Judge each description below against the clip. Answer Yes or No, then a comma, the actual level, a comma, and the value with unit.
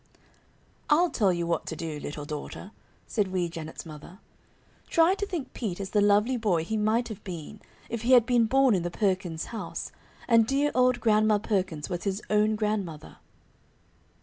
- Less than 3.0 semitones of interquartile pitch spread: No, average, 5.1 semitones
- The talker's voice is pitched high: Yes, high, 210 Hz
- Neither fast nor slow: Yes, average, 175 wpm